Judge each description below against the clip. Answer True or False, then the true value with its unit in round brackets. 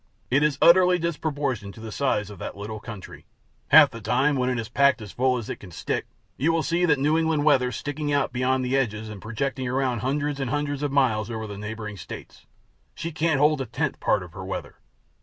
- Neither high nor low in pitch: False (130 Hz)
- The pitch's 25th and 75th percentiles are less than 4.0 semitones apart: False (4.9 semitones)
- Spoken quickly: True (225 wpm)